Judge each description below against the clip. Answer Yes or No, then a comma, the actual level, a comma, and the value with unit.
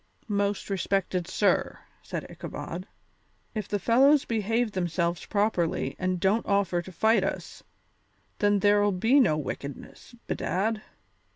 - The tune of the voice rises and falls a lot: No, average, 3.2 semitones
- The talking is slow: Yes, slow, 120 wpm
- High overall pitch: Yes, high, 200 Hz